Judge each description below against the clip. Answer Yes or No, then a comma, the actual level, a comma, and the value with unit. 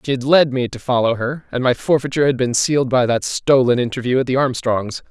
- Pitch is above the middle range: No, low, 130 Hz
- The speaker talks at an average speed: No, fast, 235 wpm